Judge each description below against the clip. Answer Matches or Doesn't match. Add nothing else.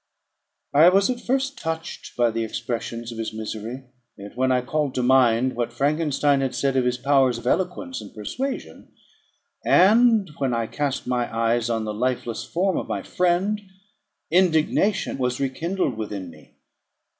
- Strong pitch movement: Matches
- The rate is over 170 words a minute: Doesn't match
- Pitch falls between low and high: Doesn't match